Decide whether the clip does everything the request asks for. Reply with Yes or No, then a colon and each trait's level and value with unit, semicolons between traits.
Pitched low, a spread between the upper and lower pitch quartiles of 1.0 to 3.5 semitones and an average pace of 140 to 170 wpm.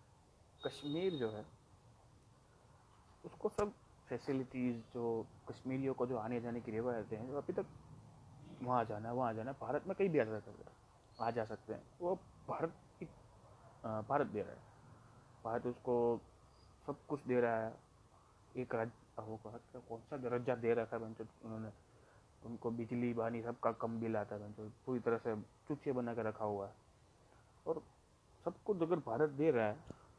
Yes: low, 115 Hz; average, 2.8 semitones; average, 165 wpm